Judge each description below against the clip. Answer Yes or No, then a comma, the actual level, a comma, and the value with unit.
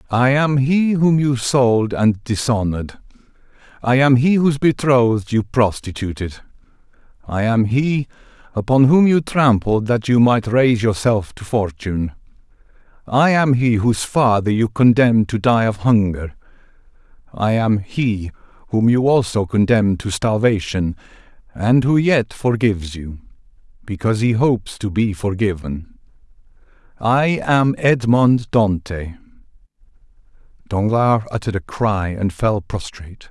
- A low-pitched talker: Yes, low, 115 Hz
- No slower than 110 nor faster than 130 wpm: Yes, slow, 120 wpm